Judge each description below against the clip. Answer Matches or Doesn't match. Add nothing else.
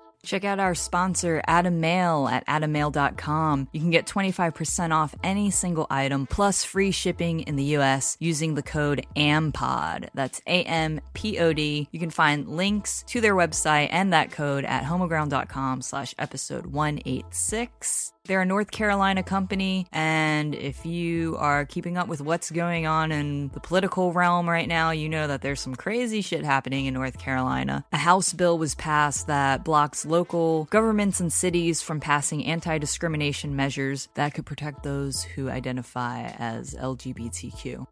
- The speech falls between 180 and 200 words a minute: Doesn't match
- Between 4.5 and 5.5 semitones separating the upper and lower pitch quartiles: Doesn't match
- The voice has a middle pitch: Matches